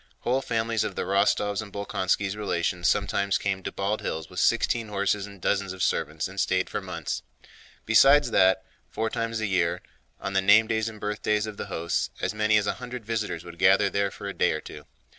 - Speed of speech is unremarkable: No, fast, 210 wpm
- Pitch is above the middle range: No, low, 100 Hz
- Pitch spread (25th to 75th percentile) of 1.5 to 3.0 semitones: Yes, narrow, 2.5 semitones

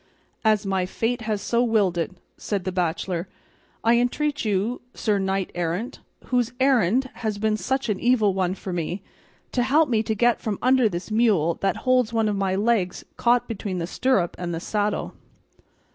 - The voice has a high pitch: Yes, high, 215 Hz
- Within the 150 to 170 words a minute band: No, average, 180 wpm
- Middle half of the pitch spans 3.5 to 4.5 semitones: Yes, average, 4.2 semitones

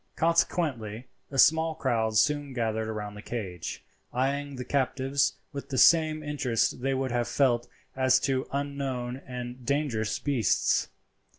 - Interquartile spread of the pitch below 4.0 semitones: Yes, average, 3.1 semitones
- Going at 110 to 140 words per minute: Yes, slow, 135 wpm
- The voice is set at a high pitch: No, low, 130 Hz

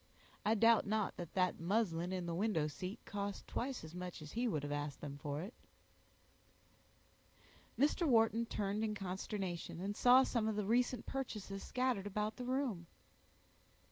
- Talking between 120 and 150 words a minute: No, average, 165 wpm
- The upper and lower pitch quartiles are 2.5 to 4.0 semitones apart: No, average, 4.6 semitones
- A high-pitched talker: Yes, high, 205 Hz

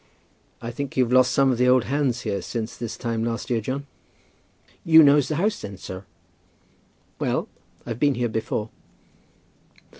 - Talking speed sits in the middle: Yes, average, 160 wpm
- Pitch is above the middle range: No, low, 125 Hz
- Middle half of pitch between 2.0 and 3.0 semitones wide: No, average, 3.4 semitones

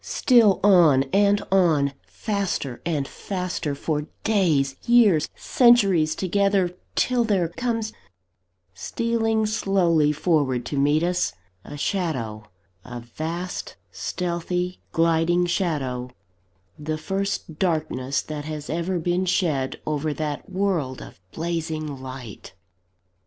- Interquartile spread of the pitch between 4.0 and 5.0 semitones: Yes, average, 4.7 semitones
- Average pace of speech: No, slow, 110 wpm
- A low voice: No, medium, 170 Hz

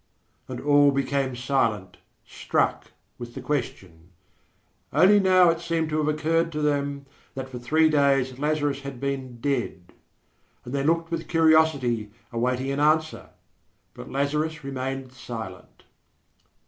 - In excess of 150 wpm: No, slow, 135 wpm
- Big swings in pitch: No, average, 3.5 semitones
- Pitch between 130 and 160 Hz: Yes, medium, 140 Hz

